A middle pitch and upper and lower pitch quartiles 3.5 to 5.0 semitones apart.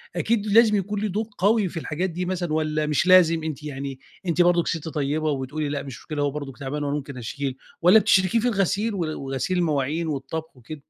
Yes: medium, 160 Hz; average, 4.5 semitones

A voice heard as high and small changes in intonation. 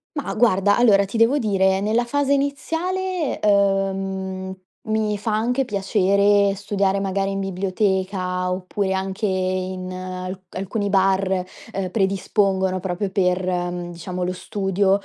Yes: high, 195 Hz; narrow, 1.9 semitones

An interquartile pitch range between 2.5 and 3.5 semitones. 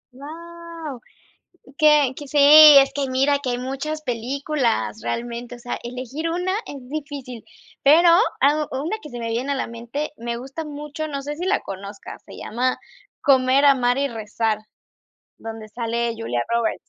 No: average, 4.0 semitones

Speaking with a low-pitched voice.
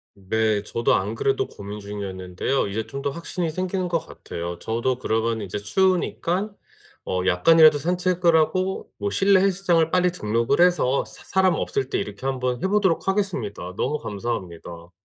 Yes: low, 130 Hz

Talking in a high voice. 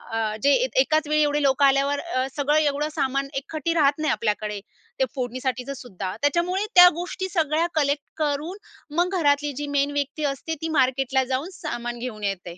Yes: very high, 285 Hz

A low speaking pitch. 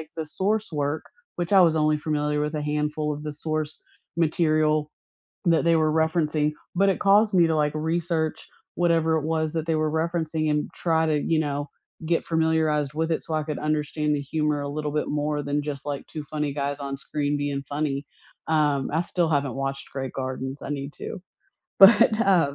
No: medium, 155 Hz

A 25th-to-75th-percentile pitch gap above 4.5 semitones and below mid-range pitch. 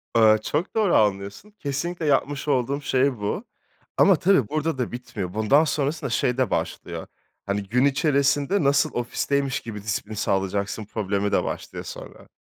Yes: wide, 5.5 semitones; low, 130 Hz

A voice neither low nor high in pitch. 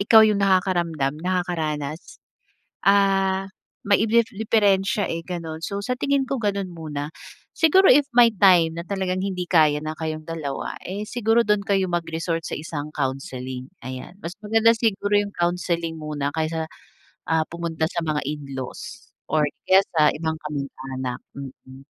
Yes: medium, 170 Hz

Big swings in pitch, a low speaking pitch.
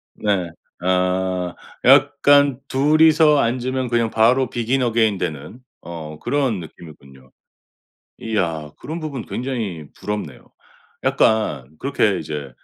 Yes: wide, 7.4 semitones; low, 110 Hz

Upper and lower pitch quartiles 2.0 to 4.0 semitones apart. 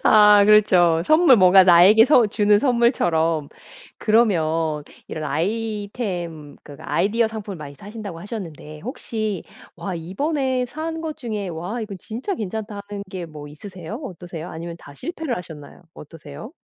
No: average, 5.3 semitones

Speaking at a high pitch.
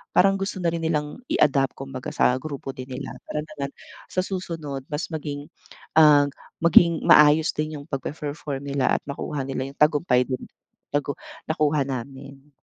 No: medium, 145 Hz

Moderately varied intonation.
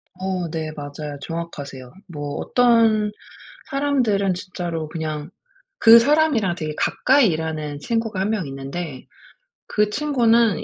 No: wide, 6.8 semitones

